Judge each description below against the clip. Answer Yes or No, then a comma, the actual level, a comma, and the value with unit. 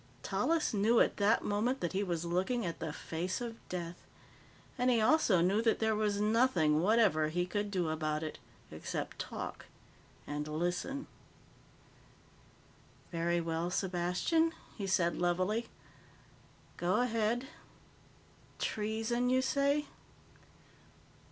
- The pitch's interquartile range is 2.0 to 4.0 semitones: No, average, 5.1 semitones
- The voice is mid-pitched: No, high, 200 Hz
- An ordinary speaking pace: No, slow, 120 wpm